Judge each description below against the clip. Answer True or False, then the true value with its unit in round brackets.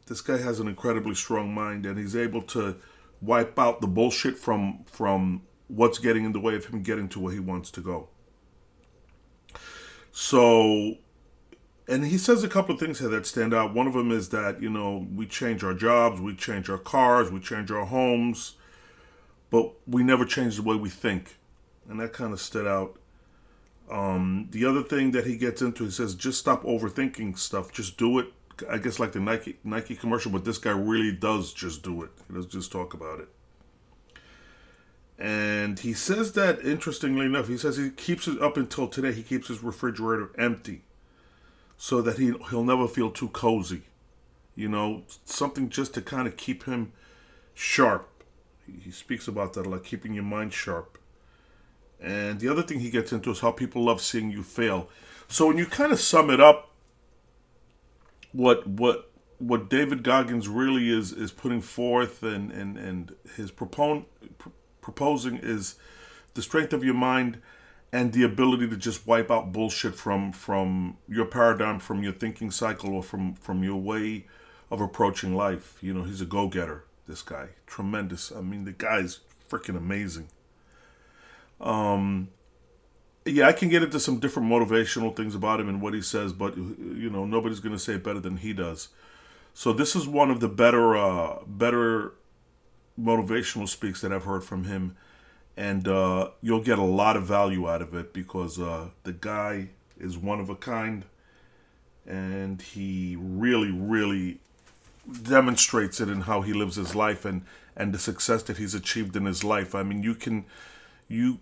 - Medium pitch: False (110 Hz)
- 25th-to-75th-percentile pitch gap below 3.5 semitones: False (3.8 semitones)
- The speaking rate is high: False (180 wpm)